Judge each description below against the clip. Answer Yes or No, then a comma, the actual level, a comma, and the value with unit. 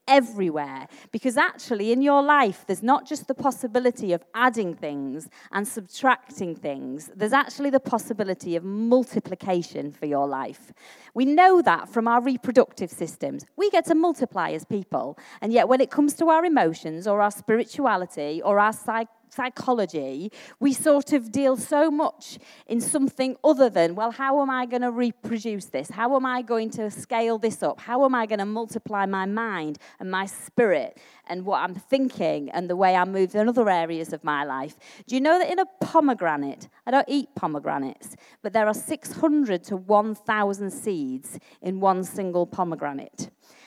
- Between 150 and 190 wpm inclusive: Yes, average, 175 wpm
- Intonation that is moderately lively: No, wide, 6.0 semitones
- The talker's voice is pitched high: Yes, high, 225 Hz